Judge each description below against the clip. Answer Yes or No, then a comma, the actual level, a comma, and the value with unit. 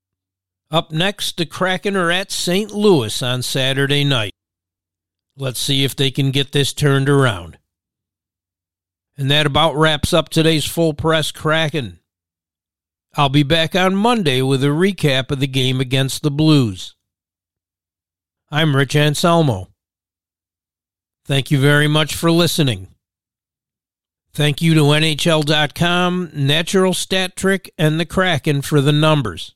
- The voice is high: No, medium, 140 Hz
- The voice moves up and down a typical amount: No, wide, 9.0 semitones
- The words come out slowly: Yes, slow, 130 wpm